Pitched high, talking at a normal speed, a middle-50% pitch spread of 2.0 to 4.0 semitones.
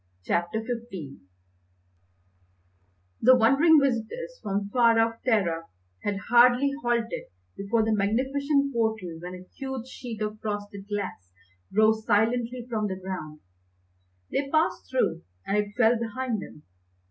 No: high, 225 Hz; slow, 125 wpm; average, 3.7 semitones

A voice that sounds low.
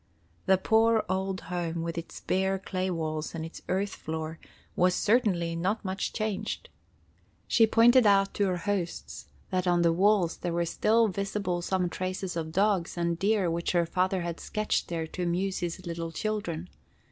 No: medium, 185 Hz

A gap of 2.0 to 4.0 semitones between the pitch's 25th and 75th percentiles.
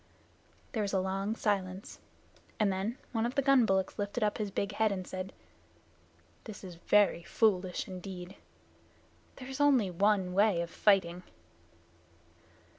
Yes: narrow, 2.6 semitones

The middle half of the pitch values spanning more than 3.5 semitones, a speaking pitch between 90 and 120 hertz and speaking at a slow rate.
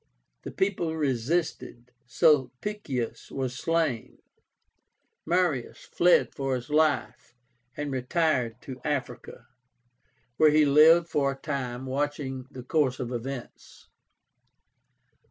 No: average, 3.9 semitones; medium, 140 Hz; slow, 100 wpm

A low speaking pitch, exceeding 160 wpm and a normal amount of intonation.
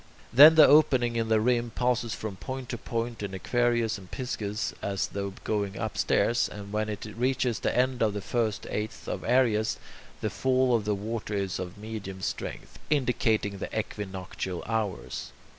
Yes: low, 110 Hz; average, 170 wpm; average, 3.2 semitones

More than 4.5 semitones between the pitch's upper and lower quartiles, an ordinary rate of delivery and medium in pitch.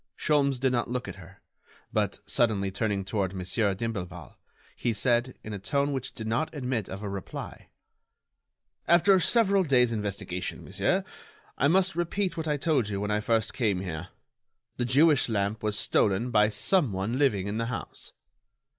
No: wide, 5.6 semitones; average, 170 wpm; low, 115 Hz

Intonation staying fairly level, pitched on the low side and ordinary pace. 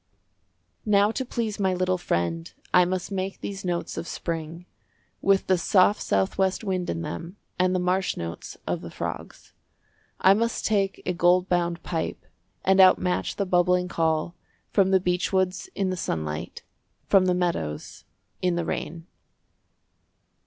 No: narrow, 2.0 semitones; medium, 180 Hz; average, 150 wpm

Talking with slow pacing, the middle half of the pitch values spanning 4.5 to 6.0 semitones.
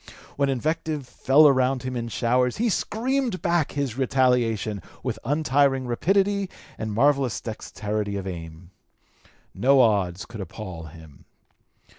Yes: slow, 125 wpm; average, 5.3 semitones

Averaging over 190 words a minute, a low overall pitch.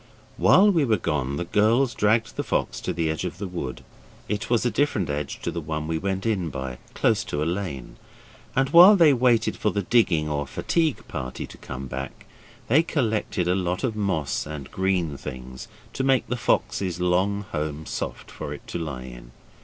Yes: average, 200 wpm; very low, 90 Hz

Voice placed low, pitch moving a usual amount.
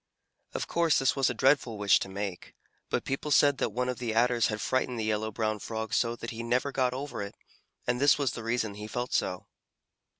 Yes: low, 120 Hz; average, 3.1 semitones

